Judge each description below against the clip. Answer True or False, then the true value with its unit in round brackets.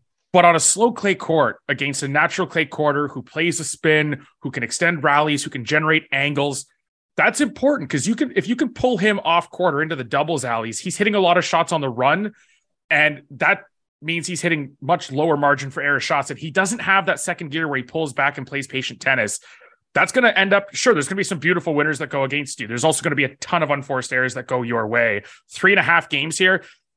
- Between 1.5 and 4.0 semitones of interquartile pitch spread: False (4.4 semitones)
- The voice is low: False (155 Hz)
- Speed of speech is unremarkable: False (245 wpm)